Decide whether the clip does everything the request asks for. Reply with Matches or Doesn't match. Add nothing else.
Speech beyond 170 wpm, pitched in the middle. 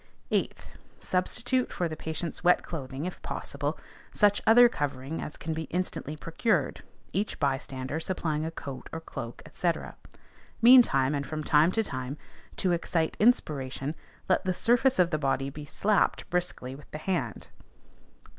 Doesn't match